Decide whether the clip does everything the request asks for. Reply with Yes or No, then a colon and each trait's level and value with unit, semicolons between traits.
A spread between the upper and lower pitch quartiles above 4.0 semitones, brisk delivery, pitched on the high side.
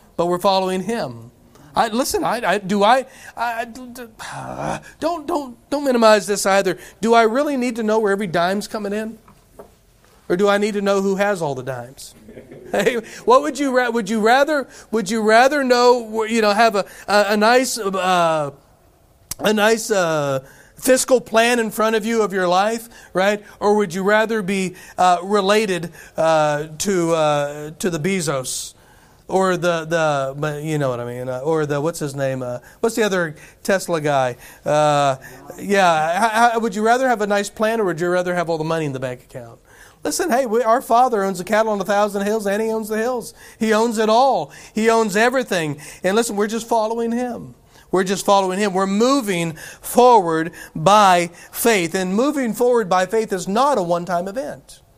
No: average, 5.3 semitones; average, 190 wpm; high, 200 Hz